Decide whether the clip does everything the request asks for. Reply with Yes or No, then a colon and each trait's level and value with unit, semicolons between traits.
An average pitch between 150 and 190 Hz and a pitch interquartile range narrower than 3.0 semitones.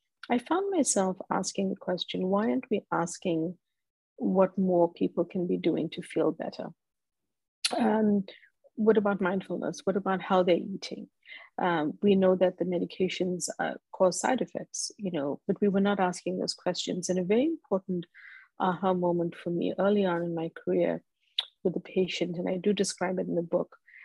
Yes: medium, 185 Hz; narrow, 2.4 semitones